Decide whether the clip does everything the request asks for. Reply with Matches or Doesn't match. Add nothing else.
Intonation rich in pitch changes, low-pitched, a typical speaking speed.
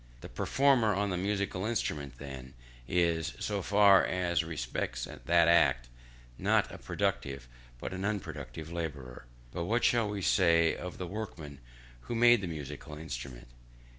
Matches